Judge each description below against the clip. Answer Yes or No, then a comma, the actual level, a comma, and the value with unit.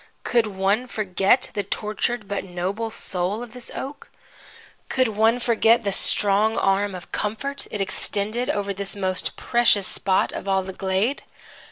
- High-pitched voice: Yes, high, 205 Hz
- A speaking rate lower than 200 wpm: Yes, average, 155 wpm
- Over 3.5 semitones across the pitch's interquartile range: No, average, 2.9 semitones